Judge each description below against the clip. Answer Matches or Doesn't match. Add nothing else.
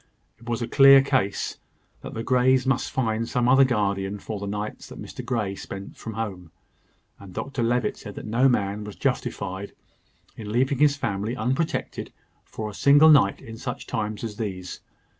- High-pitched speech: Doesn't match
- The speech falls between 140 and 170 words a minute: Doesn't match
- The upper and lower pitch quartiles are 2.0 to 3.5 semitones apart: Doesn't match